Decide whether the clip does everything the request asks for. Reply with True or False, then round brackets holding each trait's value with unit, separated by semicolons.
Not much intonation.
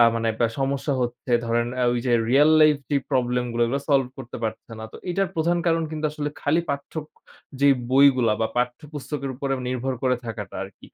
False (3.3 semitones)